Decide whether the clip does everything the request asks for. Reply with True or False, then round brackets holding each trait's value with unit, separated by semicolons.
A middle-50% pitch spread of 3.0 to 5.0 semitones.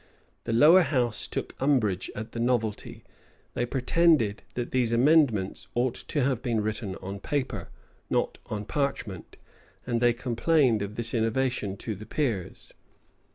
True (3.6 semitones)